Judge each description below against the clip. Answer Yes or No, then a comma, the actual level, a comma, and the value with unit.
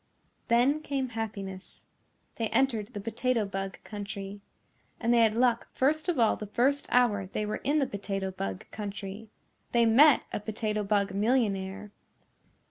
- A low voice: No, high, 215 Hz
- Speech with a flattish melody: No, average, 3.6 semitones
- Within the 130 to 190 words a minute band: Yes, average, 150 wpm